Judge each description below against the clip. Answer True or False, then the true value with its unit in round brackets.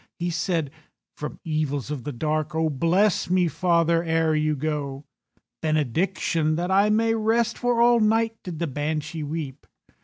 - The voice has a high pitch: False (160 Hz)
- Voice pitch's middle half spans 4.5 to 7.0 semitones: False (3.8 semitones)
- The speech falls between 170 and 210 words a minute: False (155 wpm)